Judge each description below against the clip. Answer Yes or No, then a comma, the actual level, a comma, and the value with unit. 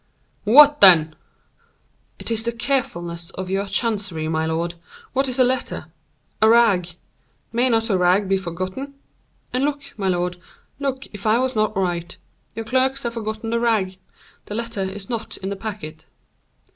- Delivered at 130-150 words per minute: No, average, 165 wpm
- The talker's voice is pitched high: Yes, high, 215 Hz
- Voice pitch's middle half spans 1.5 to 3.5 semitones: No, average, 4.3 semitones